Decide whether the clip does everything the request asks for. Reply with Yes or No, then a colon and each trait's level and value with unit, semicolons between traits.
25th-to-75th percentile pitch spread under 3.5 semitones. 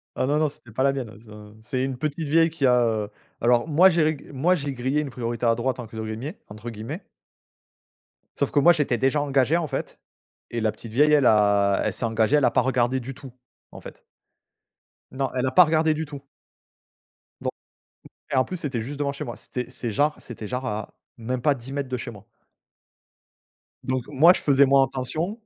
No: average, 3.8 semitones